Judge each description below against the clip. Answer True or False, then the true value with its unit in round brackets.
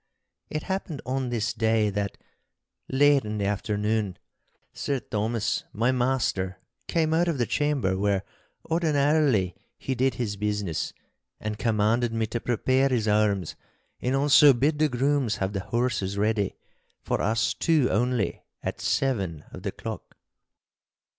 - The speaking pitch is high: False (115 Hz)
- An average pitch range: True (4.7 semitones)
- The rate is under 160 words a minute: True (140 wpm)